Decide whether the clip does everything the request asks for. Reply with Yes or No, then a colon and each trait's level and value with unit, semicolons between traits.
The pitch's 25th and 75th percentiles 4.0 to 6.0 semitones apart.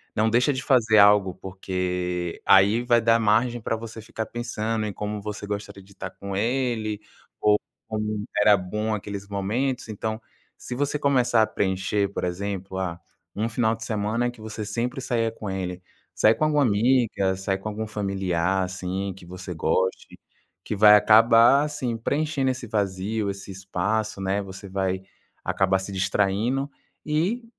No: average, 3.2 semitones